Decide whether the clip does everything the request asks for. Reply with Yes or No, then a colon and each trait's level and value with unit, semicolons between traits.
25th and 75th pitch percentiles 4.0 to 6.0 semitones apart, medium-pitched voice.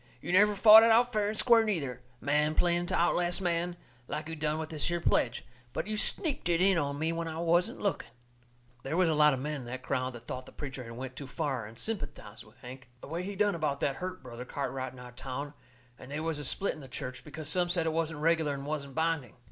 Yes: average, 4.7 semitones; medium, 155 Hz